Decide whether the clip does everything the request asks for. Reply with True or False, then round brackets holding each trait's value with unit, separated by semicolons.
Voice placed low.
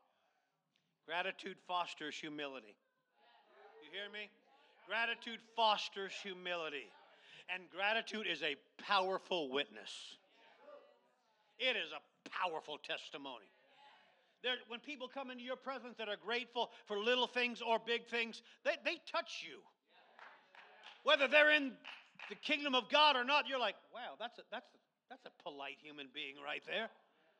False (225 Hz)